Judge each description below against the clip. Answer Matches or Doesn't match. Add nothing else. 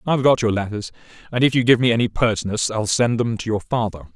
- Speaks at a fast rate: Matches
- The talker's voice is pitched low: Matches